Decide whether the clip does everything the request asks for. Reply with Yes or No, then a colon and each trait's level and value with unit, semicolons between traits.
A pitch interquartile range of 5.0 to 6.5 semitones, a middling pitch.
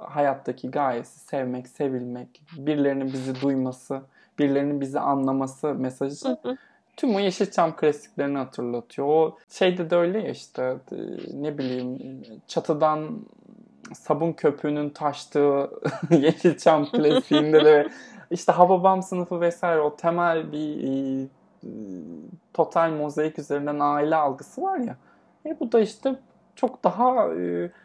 No: average, 4.5 semitones; medium, 150 Hz